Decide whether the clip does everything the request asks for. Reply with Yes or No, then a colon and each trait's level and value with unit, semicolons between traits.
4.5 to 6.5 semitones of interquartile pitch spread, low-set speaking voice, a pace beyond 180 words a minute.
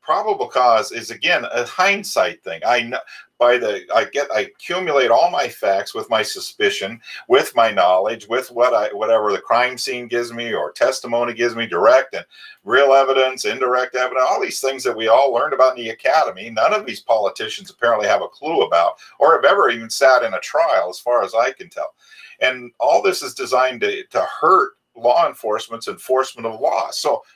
No: average, 3.5 semitones; low, 130 Hz; average, 195 wpm